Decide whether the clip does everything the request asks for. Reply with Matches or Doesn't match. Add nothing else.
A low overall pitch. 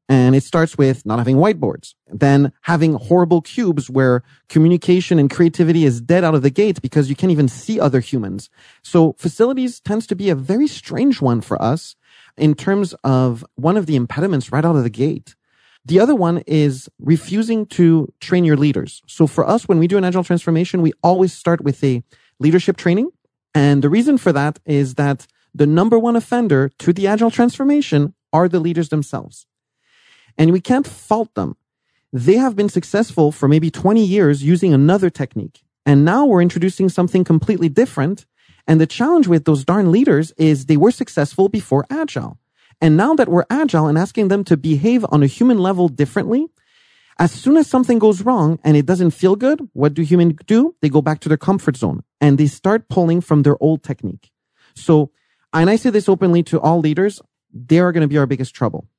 Doesn't match